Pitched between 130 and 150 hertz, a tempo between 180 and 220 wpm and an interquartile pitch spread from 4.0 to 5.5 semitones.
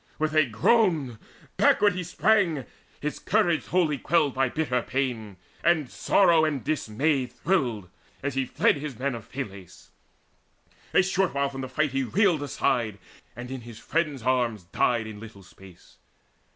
No: low, 135 Hz; average, 155 wpm; average, 5.2 semitones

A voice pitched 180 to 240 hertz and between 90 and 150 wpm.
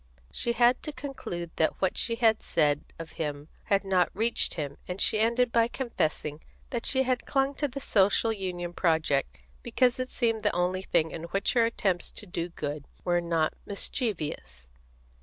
No: high, 190 Hz; average, 175 wpm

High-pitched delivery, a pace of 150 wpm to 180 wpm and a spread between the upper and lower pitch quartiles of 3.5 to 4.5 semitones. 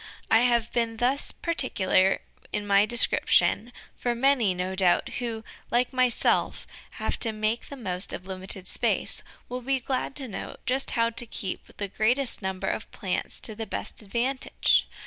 Yes: high, 230 Hz; average, 165 wpm; average, 3.9 semitones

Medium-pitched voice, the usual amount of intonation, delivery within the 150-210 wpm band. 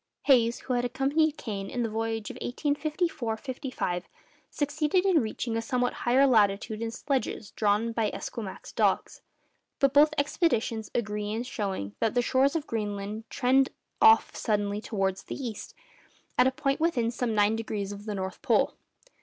No: high, 230 Hz; average, 4.4 semitones; average, 160 wpm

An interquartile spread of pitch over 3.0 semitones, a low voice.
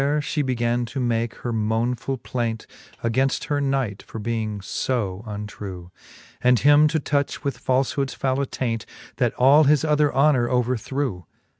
Yes: average, 3.6 semitones; low, 125 Hz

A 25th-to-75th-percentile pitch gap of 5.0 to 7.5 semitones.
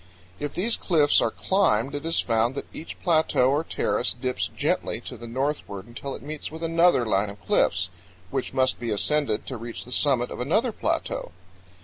Yes: wide, 5.4 semitones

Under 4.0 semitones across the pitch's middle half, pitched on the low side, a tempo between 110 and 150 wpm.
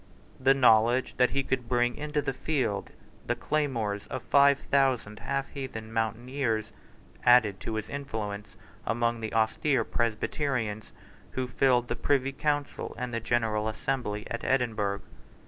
Yes: average, 3.6 semitones; low, 120 Hz; average, 140 wpm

